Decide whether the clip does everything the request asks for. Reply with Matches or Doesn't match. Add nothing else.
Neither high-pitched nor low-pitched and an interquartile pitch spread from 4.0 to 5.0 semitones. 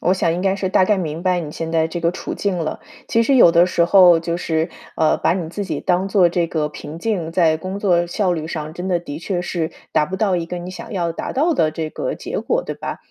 Doesn't match